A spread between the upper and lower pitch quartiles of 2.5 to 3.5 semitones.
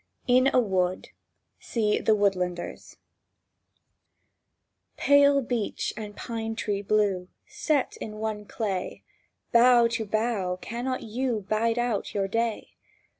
Yes: average, 2.9 semitones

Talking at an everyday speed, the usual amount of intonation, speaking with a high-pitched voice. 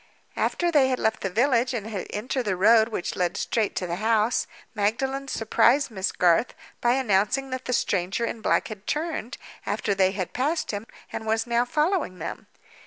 Yes: average, 185 wpm; average, 4.2 semitones; high, 225 Hz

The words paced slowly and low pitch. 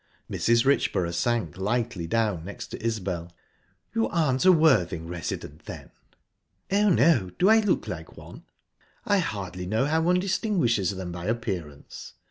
No: average, 145 wpm; low, 115 Hz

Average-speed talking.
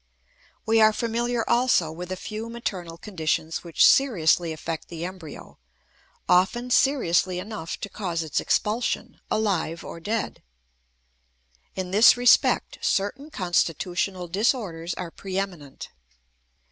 No: slow, 115 wpm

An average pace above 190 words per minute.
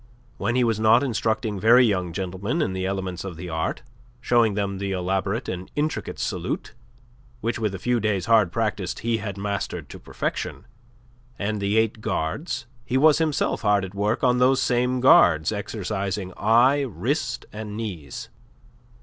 No: average, 165 wpm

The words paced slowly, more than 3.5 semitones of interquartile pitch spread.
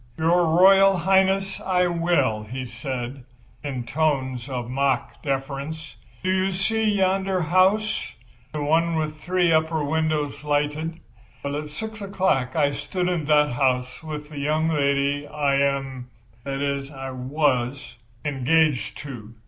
Yes: slow, 130 wpm; average, 4.0 semitones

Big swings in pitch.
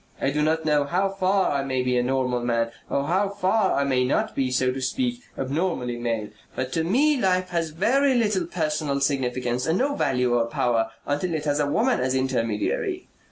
Yes: wide, 6.4 semitones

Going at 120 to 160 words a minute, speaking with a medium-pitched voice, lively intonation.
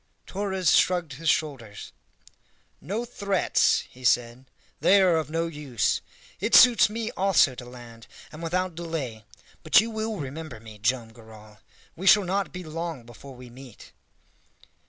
Yes: average, 150 wpm; medium, 155 Hz; wide, 7.3 semitones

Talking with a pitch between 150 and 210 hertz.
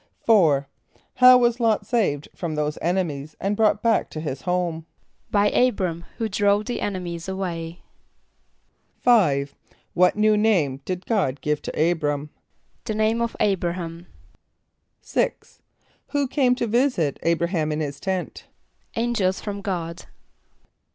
Yes: medium, 185 Hz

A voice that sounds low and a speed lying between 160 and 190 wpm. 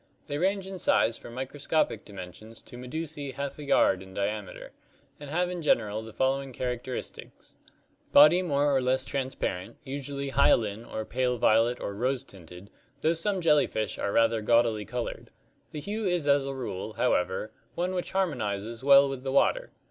Yes: low, 130 Hz; average, 165 wpm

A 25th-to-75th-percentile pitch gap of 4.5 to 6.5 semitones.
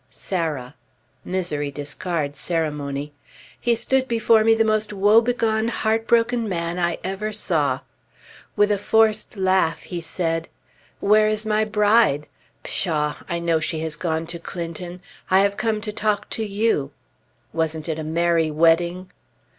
Yes: average, 4.9 semitones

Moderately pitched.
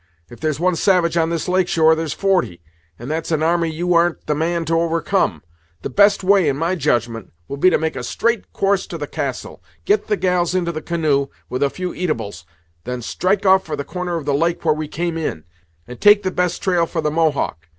Yes: medium, 165 Hz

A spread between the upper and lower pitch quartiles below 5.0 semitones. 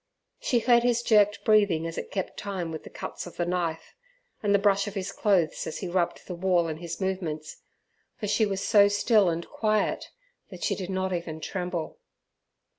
Yes: average, 3.2 semitones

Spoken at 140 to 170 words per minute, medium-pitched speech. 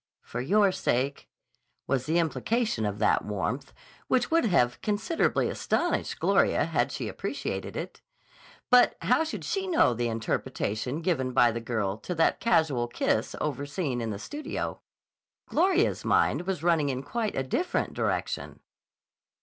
Yes: average, 145 wpm; medium, 145 Hz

